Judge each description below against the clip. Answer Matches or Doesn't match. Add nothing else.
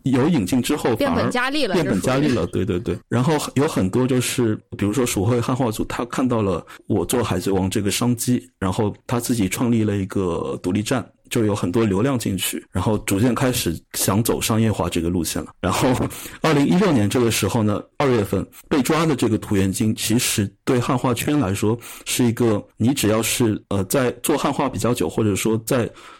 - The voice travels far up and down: Doesn't match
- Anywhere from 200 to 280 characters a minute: Doesn't match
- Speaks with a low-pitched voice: Matches